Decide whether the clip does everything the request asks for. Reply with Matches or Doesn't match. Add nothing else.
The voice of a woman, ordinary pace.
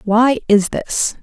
Matches